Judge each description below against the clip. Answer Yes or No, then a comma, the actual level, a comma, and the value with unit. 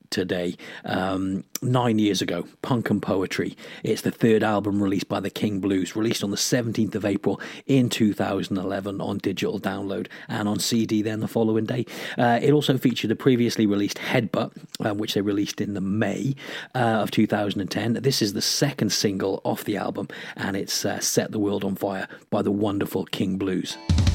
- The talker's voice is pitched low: Yes, low, 105 Hz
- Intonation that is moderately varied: No, narrow, 2.3 semitones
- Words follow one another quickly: No, average, 185 wpm